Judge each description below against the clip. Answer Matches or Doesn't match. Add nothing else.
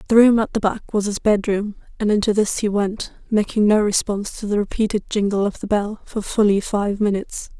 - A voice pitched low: Doesn't match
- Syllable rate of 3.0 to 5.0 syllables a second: Doesn't match